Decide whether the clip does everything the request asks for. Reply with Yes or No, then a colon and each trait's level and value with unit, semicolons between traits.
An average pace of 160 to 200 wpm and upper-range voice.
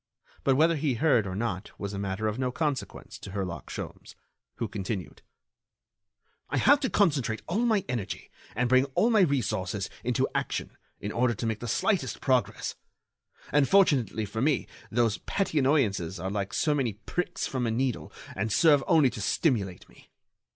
No: average, 170 wpm; low, 125 Hz